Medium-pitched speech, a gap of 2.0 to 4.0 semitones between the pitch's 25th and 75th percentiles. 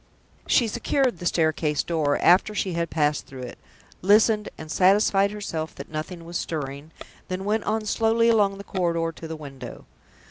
No: medium, 175 Hz; average, 4.9 semitones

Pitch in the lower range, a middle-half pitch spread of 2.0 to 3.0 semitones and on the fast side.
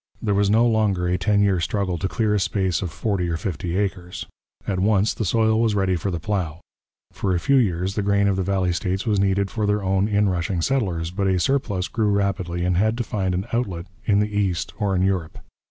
Yes: low, 100 Hz; narrow, 2.5 semitones; fast, 230 wpm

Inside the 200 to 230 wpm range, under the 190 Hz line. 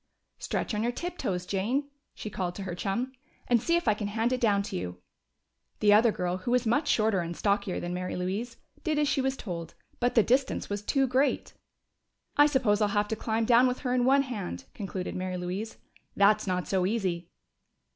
No: fast, 205 wpm; high, 215 Hz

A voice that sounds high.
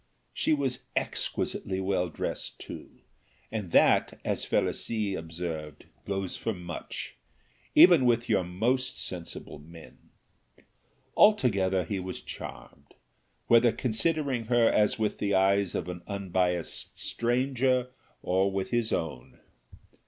No: low, 100 Hz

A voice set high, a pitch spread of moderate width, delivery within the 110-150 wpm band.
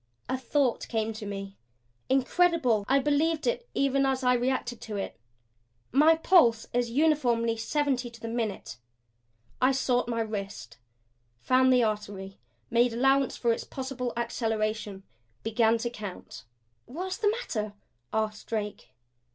Yes: high, 240 Hz; average, 3.8 semitones; slow, 135 wpm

